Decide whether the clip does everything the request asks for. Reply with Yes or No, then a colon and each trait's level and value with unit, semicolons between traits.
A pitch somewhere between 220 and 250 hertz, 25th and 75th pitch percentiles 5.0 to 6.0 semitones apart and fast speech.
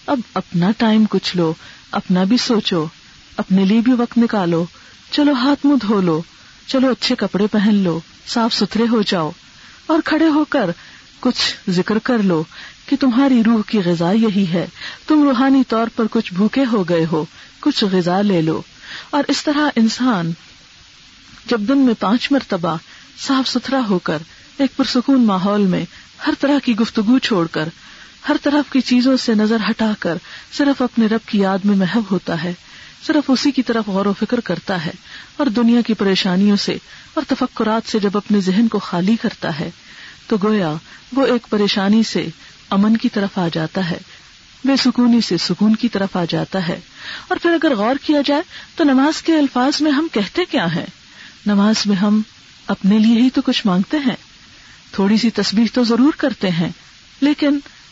No: high, 225 Hz; wide, 5.4 semitones; average, 180 wpm